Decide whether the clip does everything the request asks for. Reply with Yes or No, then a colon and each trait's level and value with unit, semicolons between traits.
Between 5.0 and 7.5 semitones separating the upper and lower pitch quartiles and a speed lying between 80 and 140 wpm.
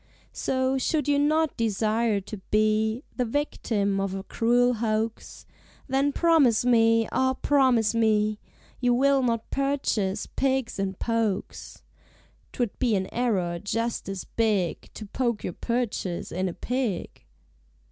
No: average, 3.7 semitones; slow, 135 wpm